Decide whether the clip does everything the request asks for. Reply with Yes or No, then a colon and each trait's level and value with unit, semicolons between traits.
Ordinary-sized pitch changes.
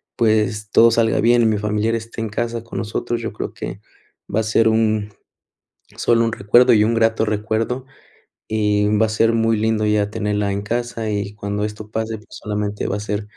No: narrow, 1.5 semitones